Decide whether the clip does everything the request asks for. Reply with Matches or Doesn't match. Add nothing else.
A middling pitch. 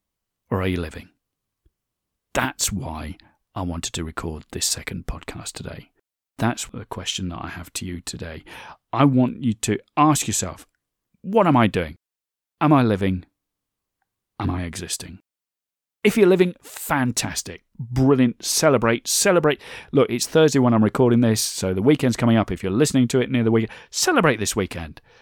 Doesn't match